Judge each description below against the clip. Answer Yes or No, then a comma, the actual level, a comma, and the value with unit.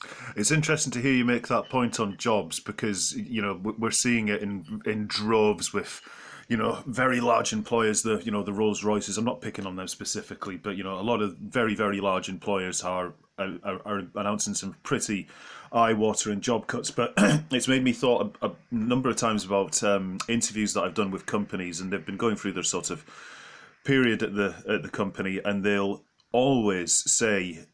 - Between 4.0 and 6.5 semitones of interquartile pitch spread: No, average, 2.9 semitones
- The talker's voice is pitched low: Yes, low, 105 Hz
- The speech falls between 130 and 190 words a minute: No, average, 200 wpm